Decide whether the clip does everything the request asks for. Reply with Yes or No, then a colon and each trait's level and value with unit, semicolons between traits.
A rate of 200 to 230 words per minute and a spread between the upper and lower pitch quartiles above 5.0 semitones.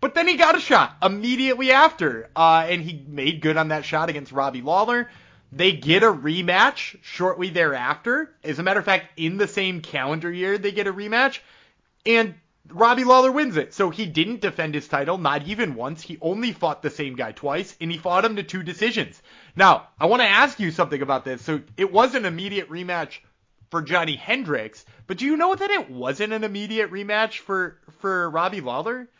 Yes: fast, 205 wpm; wide, 5.6 semitones